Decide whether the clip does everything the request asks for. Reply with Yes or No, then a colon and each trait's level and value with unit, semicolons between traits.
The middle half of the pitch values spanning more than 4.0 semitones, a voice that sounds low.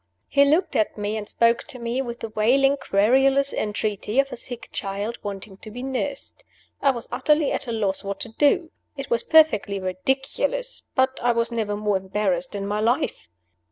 No: average, 4.7 semitones; high, 235 Hz